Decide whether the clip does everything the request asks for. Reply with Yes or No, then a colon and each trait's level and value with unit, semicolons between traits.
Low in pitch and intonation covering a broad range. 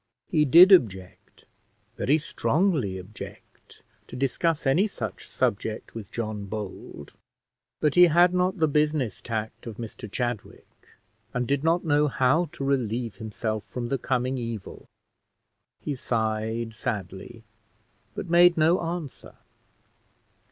Yes: low, 125 Hz; wide, 6.4 semitones